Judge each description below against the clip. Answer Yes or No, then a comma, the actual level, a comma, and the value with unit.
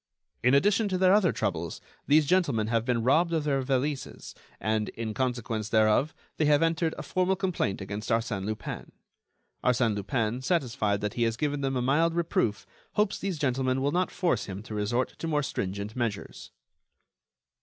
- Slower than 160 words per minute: No, average, 175 wpm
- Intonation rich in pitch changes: Yes, wide, 6.5 semitones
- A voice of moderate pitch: No, low, 130 Hz